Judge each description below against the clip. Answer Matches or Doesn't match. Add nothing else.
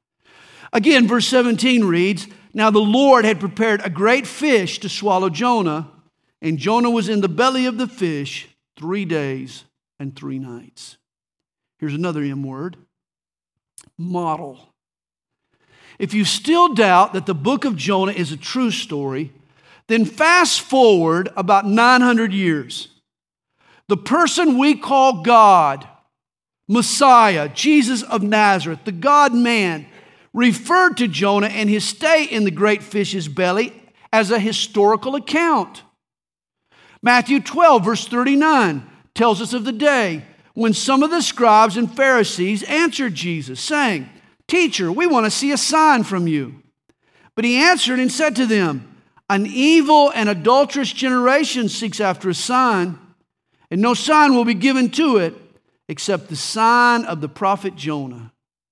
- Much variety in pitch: Matches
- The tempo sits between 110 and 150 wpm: Matches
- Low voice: Doesn't match